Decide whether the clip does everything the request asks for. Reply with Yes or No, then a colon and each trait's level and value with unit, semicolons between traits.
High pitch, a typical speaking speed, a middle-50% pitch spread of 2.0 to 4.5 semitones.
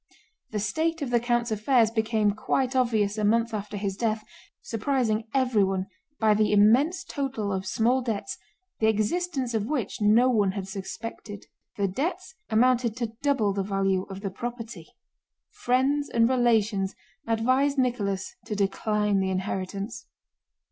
Yes: high, 220 Hz; average, 145 wpm; average, 3.7 semitones